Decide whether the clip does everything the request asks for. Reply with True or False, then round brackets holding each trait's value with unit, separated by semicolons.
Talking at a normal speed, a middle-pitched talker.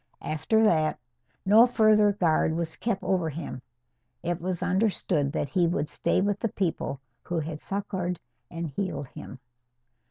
True (150 wpm; 175 Hz)